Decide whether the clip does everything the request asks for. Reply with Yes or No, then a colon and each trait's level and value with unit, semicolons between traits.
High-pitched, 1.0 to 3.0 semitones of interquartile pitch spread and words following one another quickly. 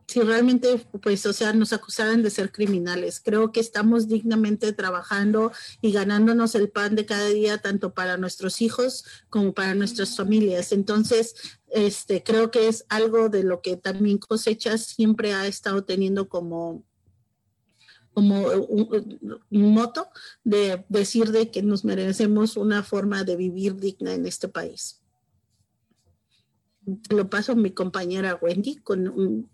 No: high, 205 Hz; narrow, 2.6 semitones; average, 150 wpm